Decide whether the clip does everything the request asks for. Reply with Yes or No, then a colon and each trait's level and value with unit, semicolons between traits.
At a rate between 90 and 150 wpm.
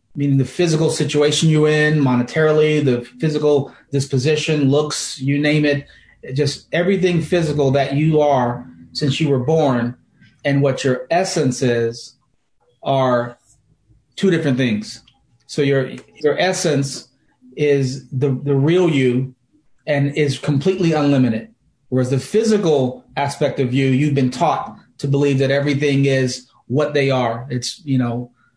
Yes: average, 140 wpm